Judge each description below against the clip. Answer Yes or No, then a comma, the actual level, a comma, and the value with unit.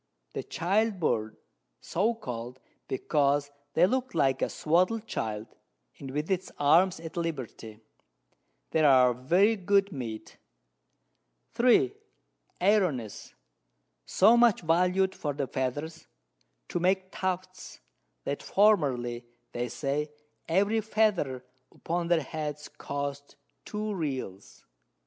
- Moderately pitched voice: Yes, medium, 160 Hz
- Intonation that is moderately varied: No, wide, 6.3 semitones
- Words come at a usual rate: No, slow, 110 wpm